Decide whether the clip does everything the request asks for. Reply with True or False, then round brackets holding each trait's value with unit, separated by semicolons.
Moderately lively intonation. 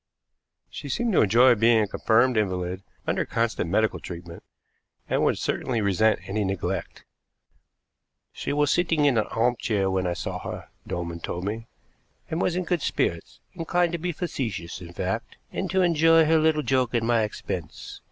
False (8.2 semitones)